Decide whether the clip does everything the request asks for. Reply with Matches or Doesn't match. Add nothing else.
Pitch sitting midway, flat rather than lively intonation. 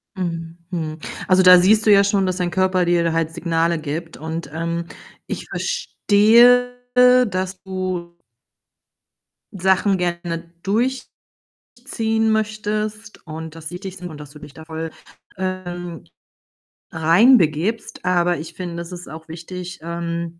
Doesn't match